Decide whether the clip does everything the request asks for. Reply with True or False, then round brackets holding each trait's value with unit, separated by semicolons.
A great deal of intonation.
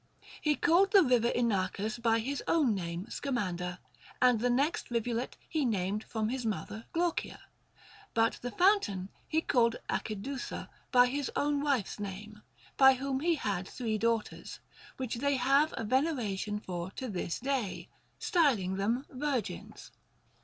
False (4.9 semitones)